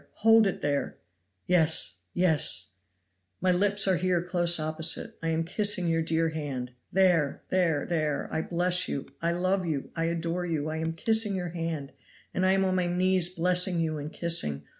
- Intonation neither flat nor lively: No, narrow, 2.3 semitones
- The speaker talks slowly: No, average, 185 wpm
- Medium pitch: Yes, medium, 170 Hz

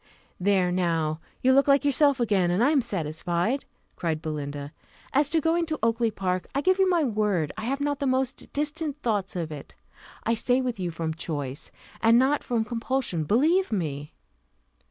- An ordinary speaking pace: Yes, average, 180 wpm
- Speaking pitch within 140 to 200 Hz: No, high, 225 Hz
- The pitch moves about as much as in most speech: No, wide, 8.3 semitones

